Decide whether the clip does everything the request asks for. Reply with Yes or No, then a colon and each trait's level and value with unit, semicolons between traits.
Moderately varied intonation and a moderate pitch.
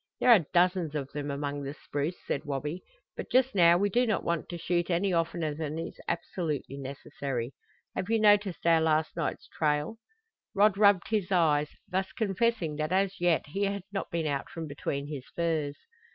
Yes: average, 4.6 semitones; medium, 170 Hz